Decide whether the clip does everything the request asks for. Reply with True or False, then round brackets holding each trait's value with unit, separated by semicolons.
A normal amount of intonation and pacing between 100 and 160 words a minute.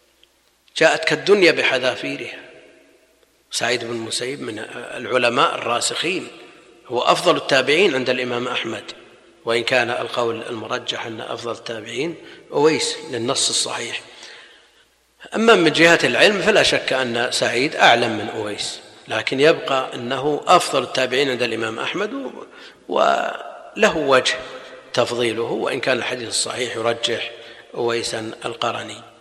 True (4.1 semitones; 110 wpm)